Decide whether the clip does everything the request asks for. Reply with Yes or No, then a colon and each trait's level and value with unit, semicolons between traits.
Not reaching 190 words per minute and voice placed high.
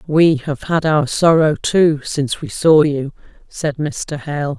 No: average, 170 wpm; medium, 150 Hz